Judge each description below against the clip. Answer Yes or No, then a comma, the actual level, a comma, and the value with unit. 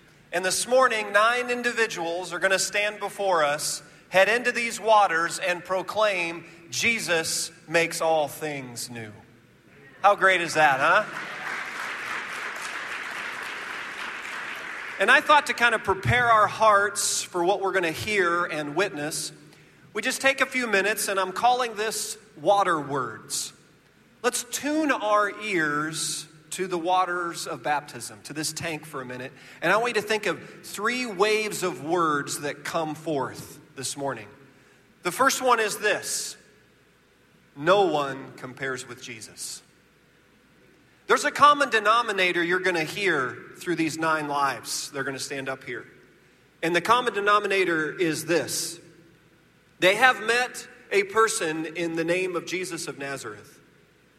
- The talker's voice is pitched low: No, medium, 175 Hz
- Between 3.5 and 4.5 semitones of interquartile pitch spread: No, wide, 5.5 semitones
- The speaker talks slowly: No, average, 145 wpm